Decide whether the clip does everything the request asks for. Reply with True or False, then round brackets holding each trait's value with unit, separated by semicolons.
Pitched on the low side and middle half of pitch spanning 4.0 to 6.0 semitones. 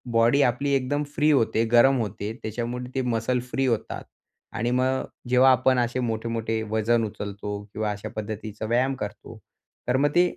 False (120 Hz; 2.9 semitones)